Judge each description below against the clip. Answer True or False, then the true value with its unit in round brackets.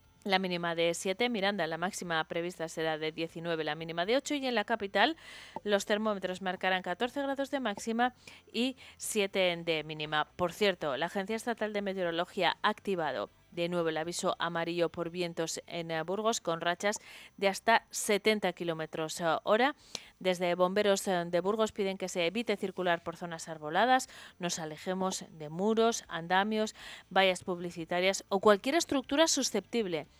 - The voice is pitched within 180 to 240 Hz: True (185 Hz)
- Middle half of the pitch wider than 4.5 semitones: False (3.8 semitones)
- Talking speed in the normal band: True (155 wpm)